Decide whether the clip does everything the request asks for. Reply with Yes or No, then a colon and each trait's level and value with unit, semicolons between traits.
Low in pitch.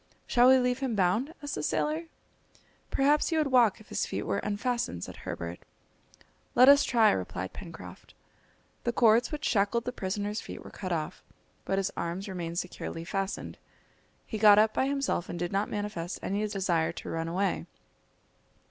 No: high, 205 Hz